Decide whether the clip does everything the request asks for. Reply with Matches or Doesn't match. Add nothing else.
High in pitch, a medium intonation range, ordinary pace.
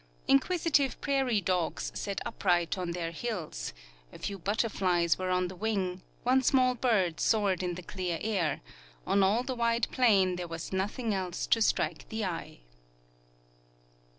Matches